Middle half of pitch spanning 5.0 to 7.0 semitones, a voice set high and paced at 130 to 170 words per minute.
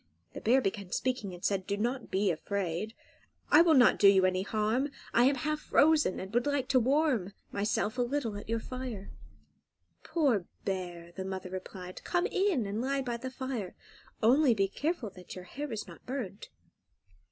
No: wide, 5.5 semitones; high, 225 Hz; average, 185 wpm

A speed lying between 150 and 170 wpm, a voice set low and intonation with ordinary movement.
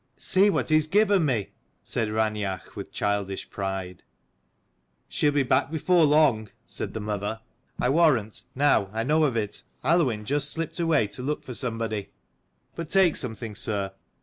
No: average, 165 wpm; low, 125 Hz; wide, 6.6 semitones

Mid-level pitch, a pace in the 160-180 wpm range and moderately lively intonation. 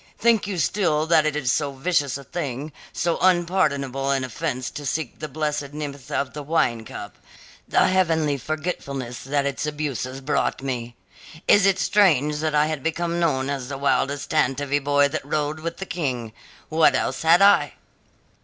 Yes: medium, 150 Hz; average, 170 wpm; average, 3.1 semitones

